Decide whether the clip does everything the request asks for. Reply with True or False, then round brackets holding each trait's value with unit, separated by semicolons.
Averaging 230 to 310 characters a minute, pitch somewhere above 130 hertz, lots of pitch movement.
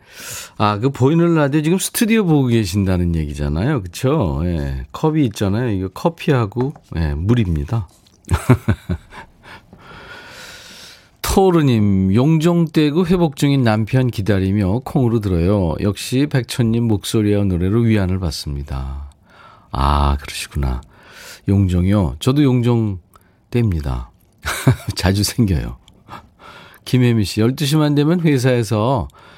False (250 characters per minute; 110 Hz; 7.0 semitones)